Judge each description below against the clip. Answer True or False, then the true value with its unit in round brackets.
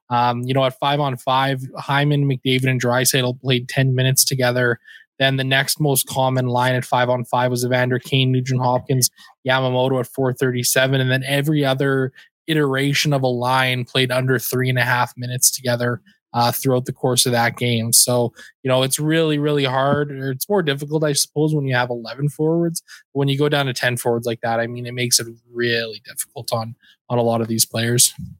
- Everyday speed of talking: False (210 wpm)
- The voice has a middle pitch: False (130 Hz)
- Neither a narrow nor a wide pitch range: False (2.0 semitones)